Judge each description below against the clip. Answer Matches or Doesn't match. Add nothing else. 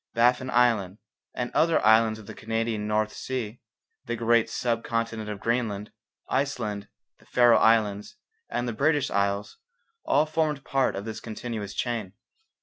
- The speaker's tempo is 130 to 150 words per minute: Matches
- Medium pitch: Doesn't match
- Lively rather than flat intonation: Doesn't match